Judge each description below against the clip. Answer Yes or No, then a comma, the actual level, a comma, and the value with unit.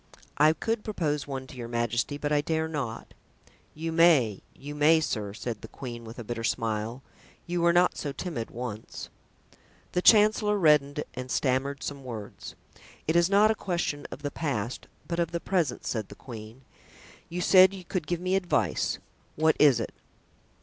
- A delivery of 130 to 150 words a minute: No, average, 175 wpm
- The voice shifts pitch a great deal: Yes, wide, 6.1 semitones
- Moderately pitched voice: Yes, medium, 145 Hz